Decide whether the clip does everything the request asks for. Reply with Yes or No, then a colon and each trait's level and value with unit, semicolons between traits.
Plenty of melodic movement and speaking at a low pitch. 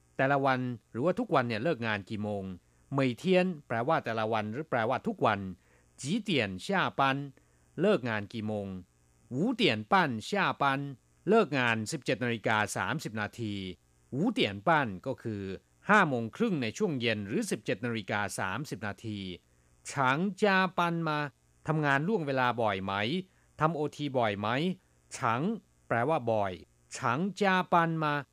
Yes: wide, 7.2 semitones; low, 120 Hz